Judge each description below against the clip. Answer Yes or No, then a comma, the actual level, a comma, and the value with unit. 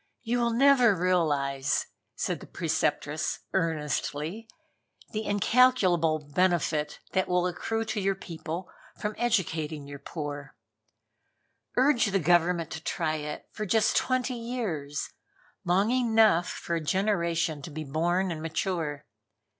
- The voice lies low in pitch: No, medium, 175 Hz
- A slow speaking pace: Yes, slow, 125 wpm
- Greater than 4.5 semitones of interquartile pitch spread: Yes, wide, 5.6 semitones